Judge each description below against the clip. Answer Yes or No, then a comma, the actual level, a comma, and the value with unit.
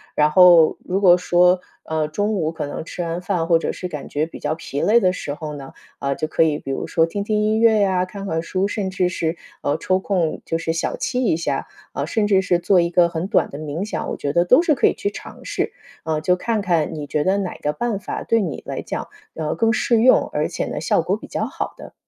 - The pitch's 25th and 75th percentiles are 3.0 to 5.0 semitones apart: Yes, average, 3.9 semitones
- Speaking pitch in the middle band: Yes, medium, 175 Hz